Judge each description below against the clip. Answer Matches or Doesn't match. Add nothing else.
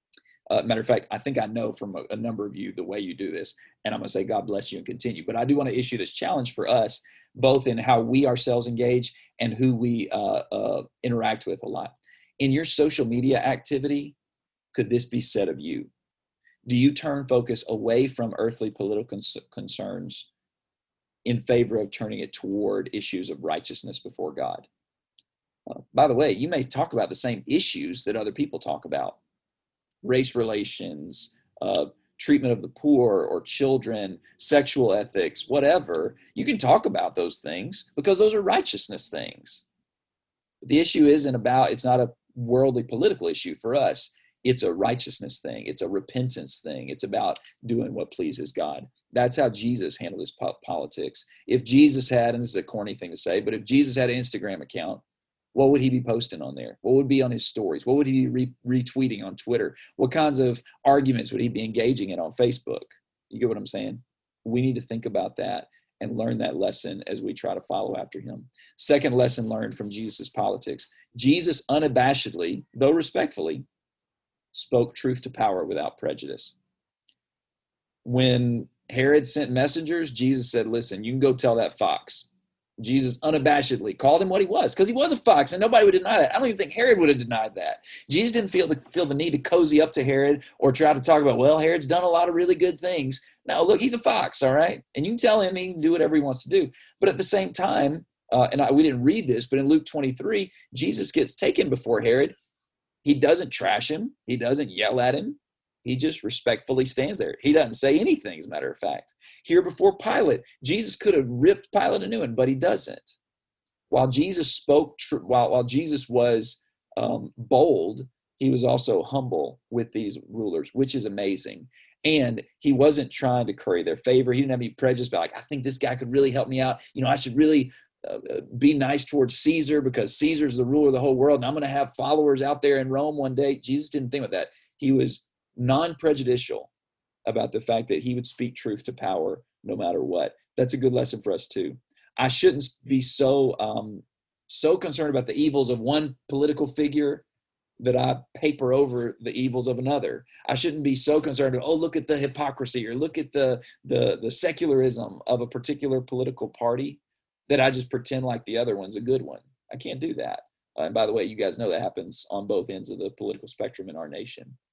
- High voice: Doesn't match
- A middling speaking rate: Doesn't match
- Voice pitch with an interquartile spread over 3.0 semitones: Matches